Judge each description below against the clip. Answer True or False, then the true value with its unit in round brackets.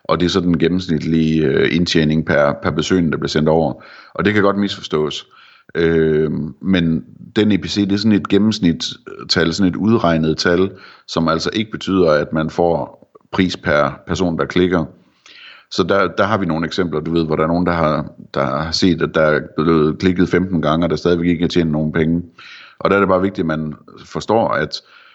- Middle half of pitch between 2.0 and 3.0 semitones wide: True (2.7 semitones)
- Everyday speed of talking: True (210 wpm)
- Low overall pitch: True (85 Hz)